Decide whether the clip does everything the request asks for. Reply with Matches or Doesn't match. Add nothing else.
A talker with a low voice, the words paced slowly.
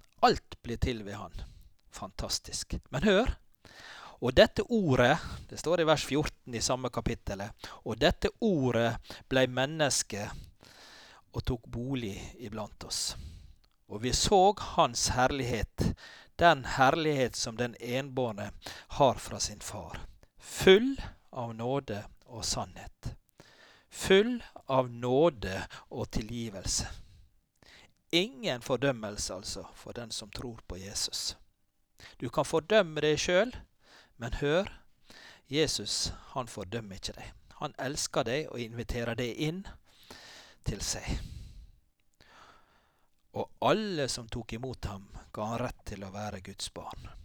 Matches